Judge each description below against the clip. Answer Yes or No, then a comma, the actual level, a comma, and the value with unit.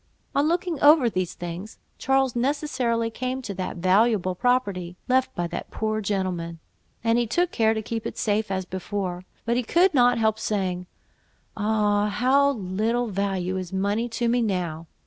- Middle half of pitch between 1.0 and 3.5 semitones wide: No, average, 4.6 semitones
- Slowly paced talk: No, average, 165 wpm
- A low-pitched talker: No, high, 215 Hz